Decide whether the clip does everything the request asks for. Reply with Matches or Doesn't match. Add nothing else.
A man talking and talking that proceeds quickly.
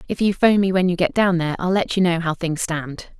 Doesn't match